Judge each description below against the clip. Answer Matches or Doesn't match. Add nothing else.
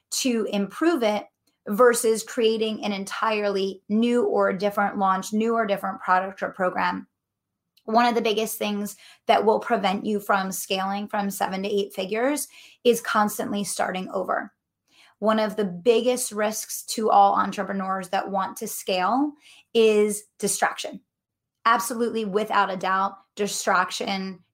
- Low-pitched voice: Doesn't match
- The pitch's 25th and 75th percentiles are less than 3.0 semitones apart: Matches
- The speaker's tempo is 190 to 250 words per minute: Doesn't match